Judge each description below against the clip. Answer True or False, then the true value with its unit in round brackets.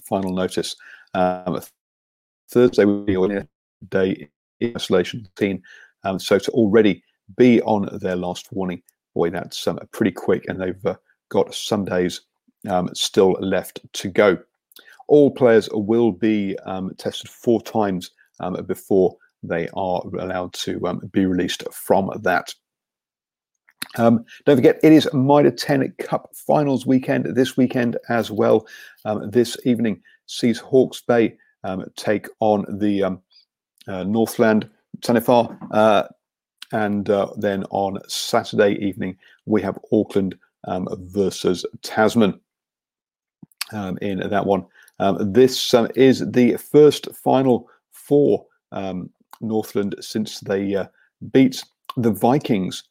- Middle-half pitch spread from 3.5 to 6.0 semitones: True (4.4 semitones)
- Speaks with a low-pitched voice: True (105 Hz)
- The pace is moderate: False (130 wpm)